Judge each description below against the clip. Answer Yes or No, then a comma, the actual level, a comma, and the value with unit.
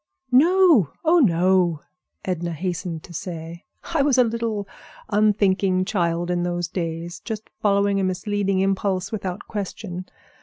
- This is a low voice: No, high, 190 Hz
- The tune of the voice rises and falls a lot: No, average, 3.2 semitones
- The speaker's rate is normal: No, slow, 130 wpm